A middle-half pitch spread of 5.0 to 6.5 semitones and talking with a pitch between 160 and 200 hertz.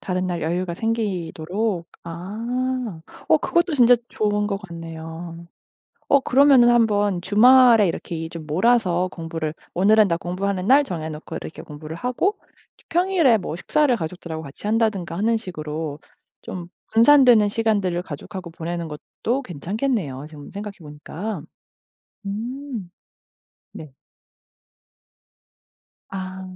Yes: wide, 5.4 semitones; high, 190 Hz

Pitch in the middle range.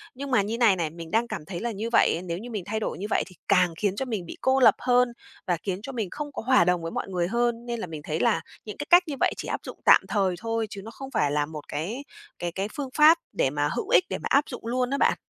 No: high, 215 Hz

